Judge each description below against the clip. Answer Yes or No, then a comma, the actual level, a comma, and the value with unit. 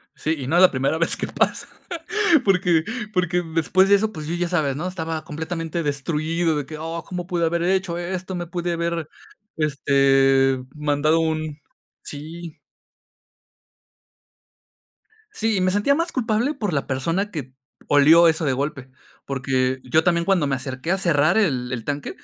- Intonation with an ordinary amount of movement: Yes, average, 3.7 semitones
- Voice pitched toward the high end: No, medium, 165 Hz